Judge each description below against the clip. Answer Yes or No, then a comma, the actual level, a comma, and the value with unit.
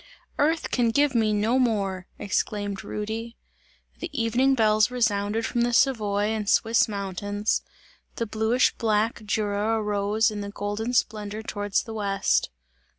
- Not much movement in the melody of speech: Yes, narrow, 2.1 semitones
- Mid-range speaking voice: No, high, 215 Hz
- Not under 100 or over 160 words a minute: Yes, slow, 135 wpm